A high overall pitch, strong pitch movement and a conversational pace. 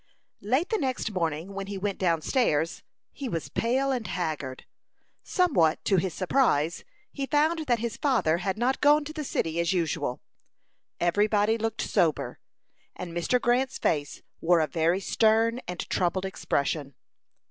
Yes: high, 195 Hz; wide, 7.0 semitones; average, 160 wpm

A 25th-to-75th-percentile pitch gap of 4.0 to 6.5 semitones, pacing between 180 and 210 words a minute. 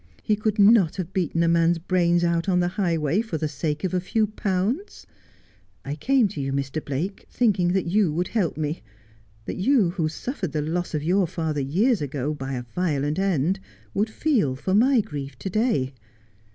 Yes: average, 4.9 semitones; average, 190 wpm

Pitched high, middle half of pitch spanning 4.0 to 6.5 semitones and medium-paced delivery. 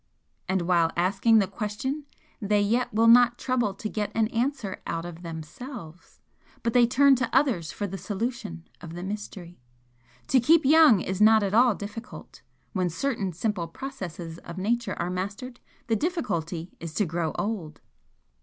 Yes: high, 205 Hz; wide, 5.4 semitones; average, 165 wpm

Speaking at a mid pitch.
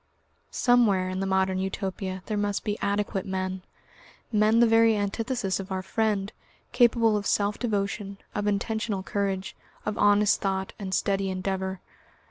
No: high, 200 Hz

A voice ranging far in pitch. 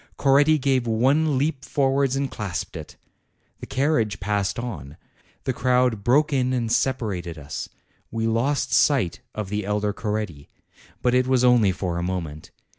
No: average, 4.9 semitones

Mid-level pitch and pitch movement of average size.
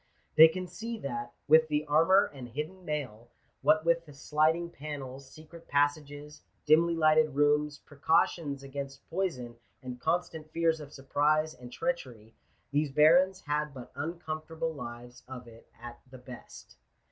Yes: medium, 150 Hz; average, 3.2 semitones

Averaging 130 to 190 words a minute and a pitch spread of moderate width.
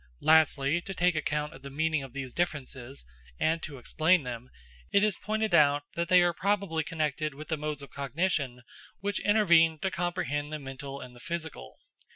Yes: average, 185 wpm; average, 3.8 semitones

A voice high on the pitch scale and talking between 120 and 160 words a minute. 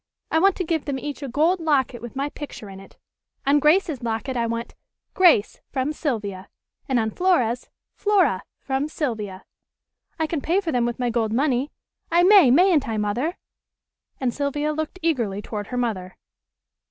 No: very high, 270 Hz; average, 175 wpm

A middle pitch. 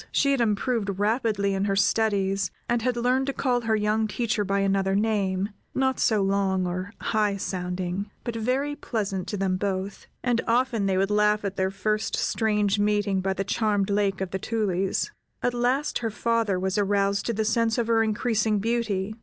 No: high, 210 Hz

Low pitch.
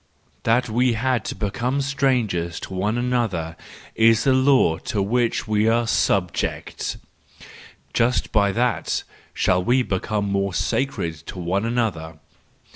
Yes: low, 110 Hz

